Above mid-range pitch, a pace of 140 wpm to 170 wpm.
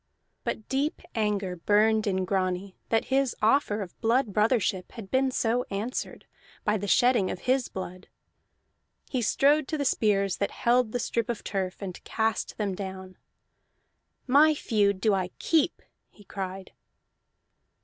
Yes: high, 215 Hz; average, 150 wpm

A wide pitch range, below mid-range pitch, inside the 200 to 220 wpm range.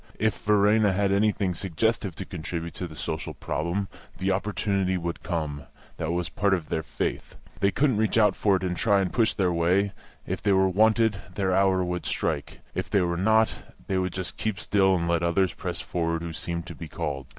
No: average, 3.0 semitones; very low, 95 Hz; fast, 205 wpm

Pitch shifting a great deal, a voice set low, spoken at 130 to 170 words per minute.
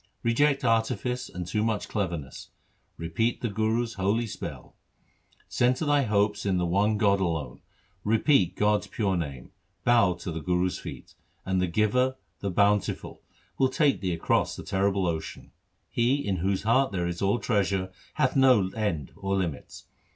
No: average, 4.3 semitones; low, 100 Hz; average, 160 wpm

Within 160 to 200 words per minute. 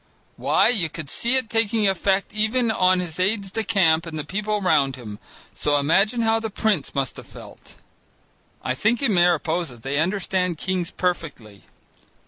Yes: average, 165 wpm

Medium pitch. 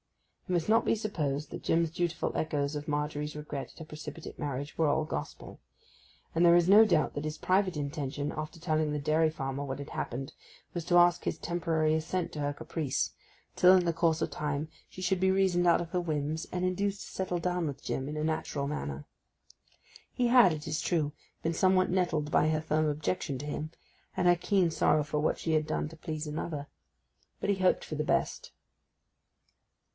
Yes: medium, 155 Hz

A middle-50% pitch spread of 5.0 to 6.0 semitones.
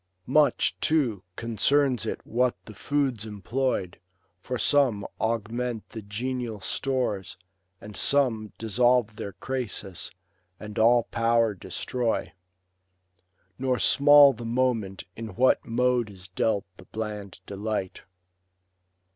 No: average, 3.4 semitones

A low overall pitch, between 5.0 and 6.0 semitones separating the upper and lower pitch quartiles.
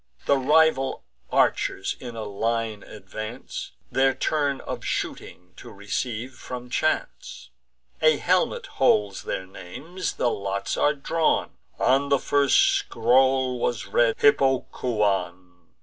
Yes: low, 125 Hz; average, 5.3 semitones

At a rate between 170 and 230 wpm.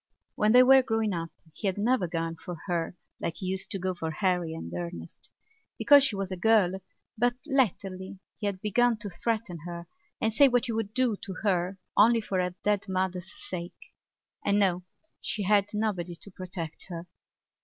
Yes: average, 185 wpm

